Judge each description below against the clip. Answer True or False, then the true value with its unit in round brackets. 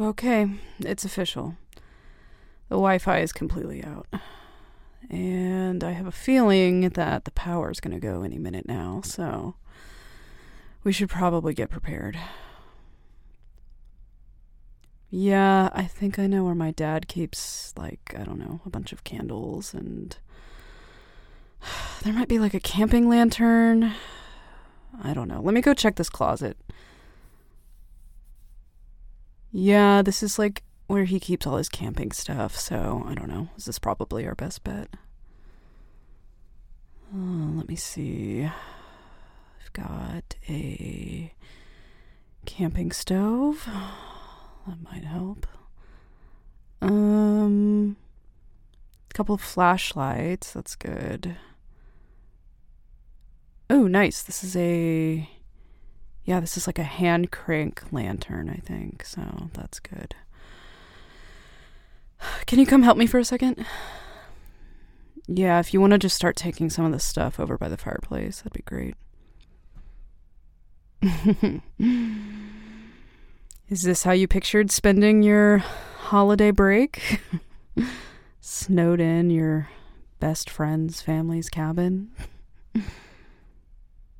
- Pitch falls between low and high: True (180 Hz)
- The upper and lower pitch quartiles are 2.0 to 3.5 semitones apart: False (5.2 semitones)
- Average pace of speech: False (115 wpm)